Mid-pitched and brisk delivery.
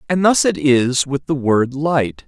Yes: medium, 145 Hz; fast, 210 wpm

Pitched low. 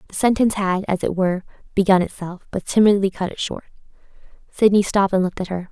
No: high, 190 Hz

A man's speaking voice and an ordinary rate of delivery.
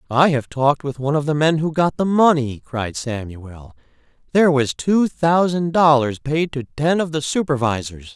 Yes: male; average, 185 wpm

